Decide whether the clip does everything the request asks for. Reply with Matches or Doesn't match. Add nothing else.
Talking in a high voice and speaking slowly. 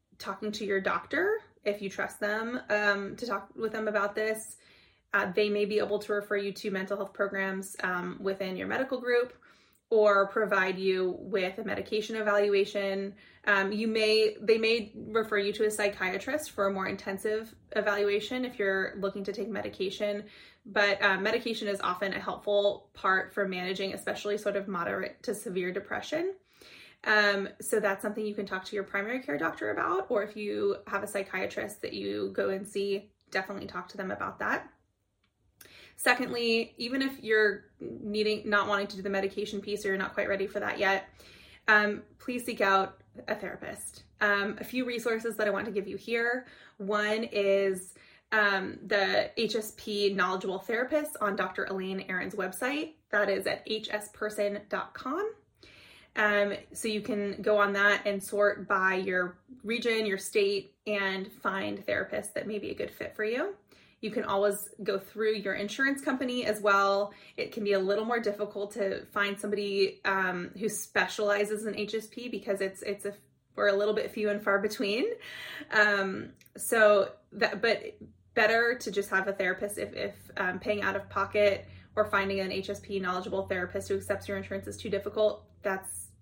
Doesn't match